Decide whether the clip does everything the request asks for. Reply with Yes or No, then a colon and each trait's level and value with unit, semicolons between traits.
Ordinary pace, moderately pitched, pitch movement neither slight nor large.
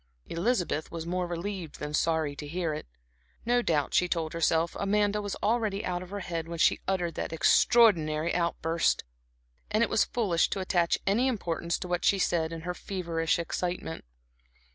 Yes: average, 175 wpm; medium, 175 Hz; average, 3.3 semitones